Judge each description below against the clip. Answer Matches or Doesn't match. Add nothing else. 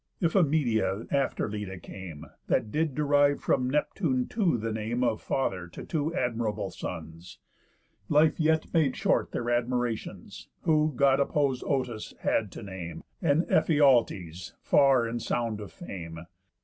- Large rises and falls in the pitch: Matches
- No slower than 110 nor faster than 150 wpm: Matches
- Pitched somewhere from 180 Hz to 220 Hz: Doesn't match